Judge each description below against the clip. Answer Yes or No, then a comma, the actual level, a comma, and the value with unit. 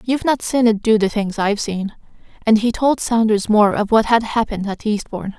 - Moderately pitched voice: No, high, 215 Hz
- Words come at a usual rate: No, fast, 225 wpm